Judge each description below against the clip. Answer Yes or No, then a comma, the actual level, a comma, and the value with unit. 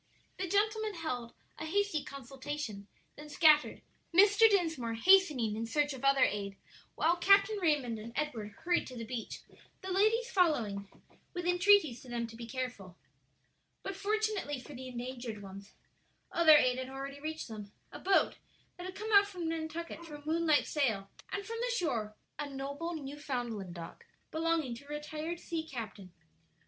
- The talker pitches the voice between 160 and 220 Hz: No, very high, 295 Hz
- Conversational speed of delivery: Yes, average, 165 wpm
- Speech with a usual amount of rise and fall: No, wide, 6.7 semitones